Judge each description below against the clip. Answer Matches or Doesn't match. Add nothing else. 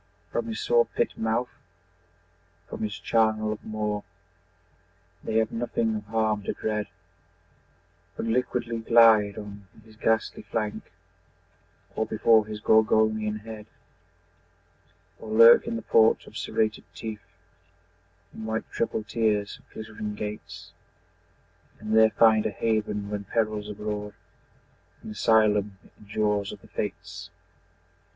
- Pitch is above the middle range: Doesn't match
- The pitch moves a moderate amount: Doesn't match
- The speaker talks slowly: Matches